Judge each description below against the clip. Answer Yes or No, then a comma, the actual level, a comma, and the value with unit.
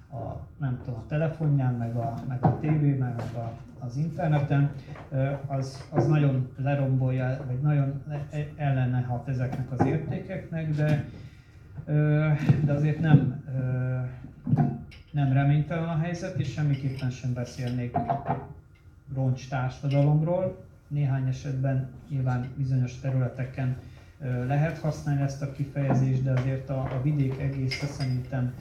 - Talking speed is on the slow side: No, average, 115 wpm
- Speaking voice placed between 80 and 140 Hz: Yes, low, 135 Hz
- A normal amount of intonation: No, narrow, 2.2 semitones